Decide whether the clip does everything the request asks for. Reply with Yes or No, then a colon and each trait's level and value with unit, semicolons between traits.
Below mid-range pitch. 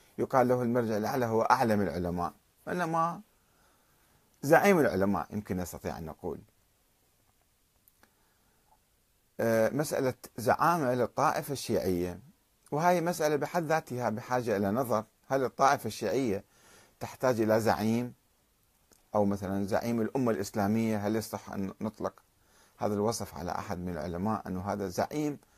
Yes: low, 110 Hz